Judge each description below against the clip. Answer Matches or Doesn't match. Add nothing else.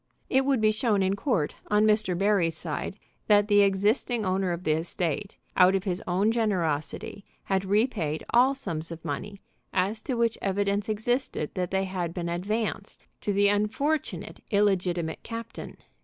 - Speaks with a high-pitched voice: Matches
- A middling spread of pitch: Matches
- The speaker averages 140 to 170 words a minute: Matches